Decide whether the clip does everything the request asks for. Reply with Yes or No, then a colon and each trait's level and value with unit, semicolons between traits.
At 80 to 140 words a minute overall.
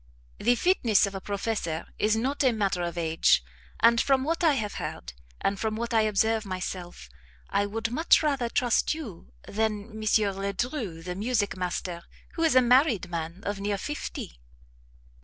No: average, 170 wpm